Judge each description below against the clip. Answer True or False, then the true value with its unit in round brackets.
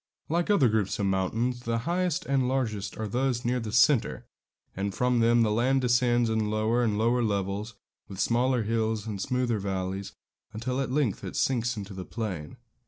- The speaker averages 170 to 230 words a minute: True (180 wpm)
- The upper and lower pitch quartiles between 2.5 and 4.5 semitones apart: True (3.1 semitones)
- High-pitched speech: False (115 Hz)